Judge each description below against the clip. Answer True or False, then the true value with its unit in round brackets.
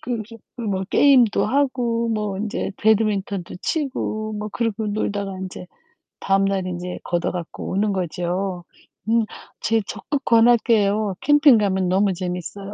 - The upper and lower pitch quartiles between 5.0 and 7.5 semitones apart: False (3.1 semitones)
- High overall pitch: True (210 Hz)